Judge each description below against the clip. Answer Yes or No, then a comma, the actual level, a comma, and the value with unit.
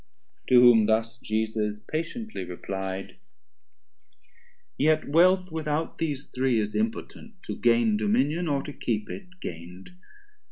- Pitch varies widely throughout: Yes, wide, 7.0 semitones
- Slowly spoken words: Yes, slow, 120 wpm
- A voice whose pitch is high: No, low, 125 Hz